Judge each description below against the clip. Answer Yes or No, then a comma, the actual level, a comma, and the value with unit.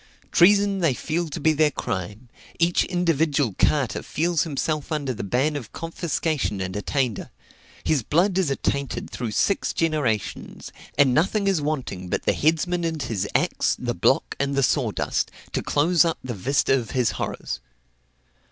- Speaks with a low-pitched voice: No, medium, 145 Hz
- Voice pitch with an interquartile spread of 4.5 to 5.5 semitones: Yes, average, 5.0 semitones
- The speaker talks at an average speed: Yes, average, 160 wpm